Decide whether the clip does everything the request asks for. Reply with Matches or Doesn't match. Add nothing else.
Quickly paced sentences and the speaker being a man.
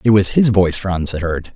Matches